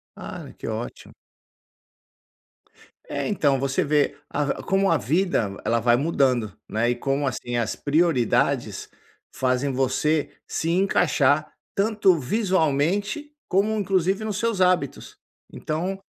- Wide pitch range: Yes, wide, 6.4 semitones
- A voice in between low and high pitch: Yes, medium, 155 Hz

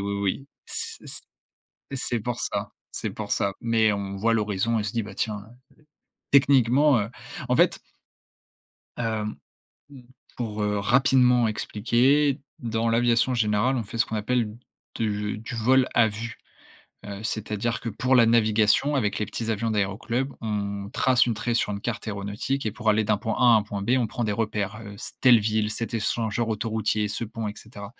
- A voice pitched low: Yes, low, 110 Hz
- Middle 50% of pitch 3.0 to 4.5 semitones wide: No, narrow, 2.4 semitones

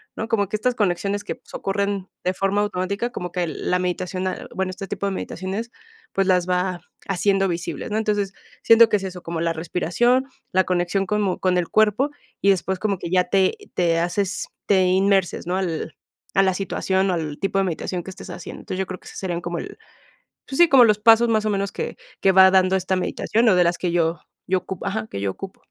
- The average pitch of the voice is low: No, high, 190 Hz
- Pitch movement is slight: Yes, narrow, 2.0 semitones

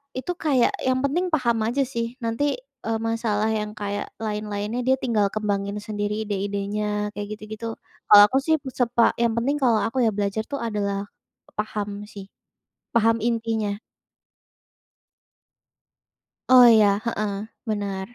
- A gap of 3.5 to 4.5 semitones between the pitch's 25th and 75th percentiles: No, narrow, 2.6 semitones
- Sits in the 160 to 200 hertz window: No, high, 220 Hz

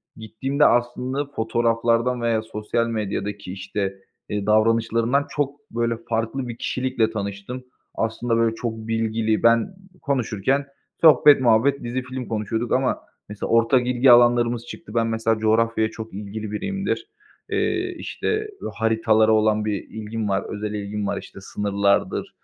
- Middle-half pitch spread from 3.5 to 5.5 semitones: No, narrow, 2.4 semitones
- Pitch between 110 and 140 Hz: Yes, low, 115 Hz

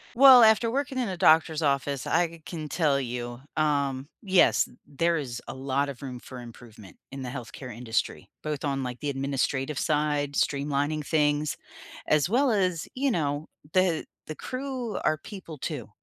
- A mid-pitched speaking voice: Yes, medium, 145 Hz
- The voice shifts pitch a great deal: No, average, 4.1 semitones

